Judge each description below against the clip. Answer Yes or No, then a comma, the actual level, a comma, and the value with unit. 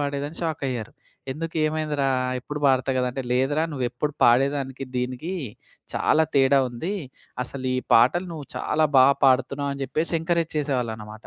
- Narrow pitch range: No, average, 3.2 semitones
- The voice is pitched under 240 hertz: Yes, medium, 140 Hz